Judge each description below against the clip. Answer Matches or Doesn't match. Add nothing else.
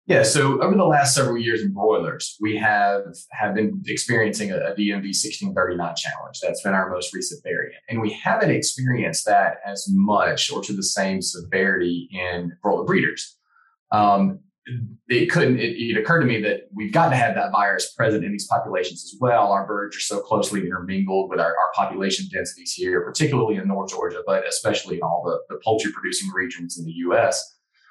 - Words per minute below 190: Doesn't match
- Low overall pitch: Matches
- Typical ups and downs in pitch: Doesn't match